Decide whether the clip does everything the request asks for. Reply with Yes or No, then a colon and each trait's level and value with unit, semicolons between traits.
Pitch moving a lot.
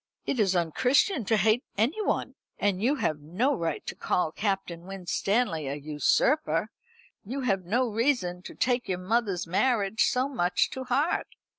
Yes: wide, 6.0 semitones